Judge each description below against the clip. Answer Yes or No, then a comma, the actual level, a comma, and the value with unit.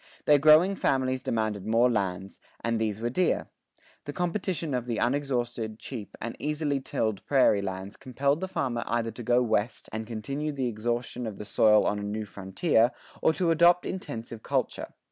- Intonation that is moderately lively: Yes, average, 4.6 semitones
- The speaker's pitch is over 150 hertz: No, low, 120 Hz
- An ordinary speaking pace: Yes, average, 175 wpm